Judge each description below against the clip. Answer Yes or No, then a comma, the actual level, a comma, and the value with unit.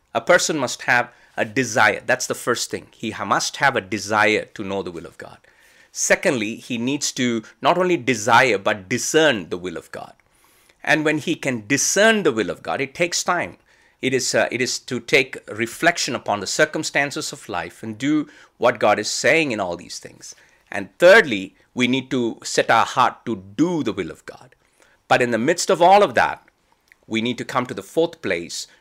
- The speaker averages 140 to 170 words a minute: No, fast, 205 wpm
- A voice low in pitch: Yes, low, 130 Hz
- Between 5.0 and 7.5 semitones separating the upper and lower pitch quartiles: Yes, wide, 5.5 semitones